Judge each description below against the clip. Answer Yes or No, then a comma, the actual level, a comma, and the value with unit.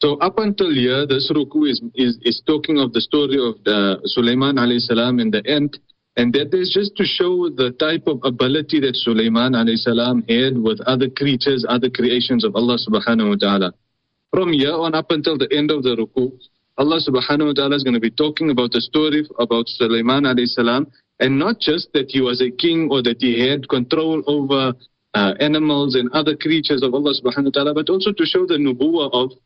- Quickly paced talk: Yes, fast, 210 wpm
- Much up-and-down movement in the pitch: No, average, 3.9 semitones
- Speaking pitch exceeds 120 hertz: Yes, low, 135 Hz